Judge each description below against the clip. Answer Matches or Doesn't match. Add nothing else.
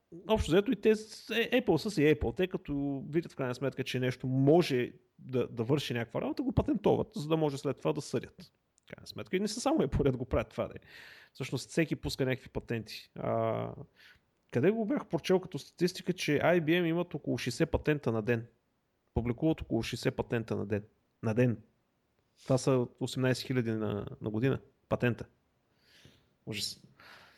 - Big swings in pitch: Matches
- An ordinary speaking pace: Doesn't match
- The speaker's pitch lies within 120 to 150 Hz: Matches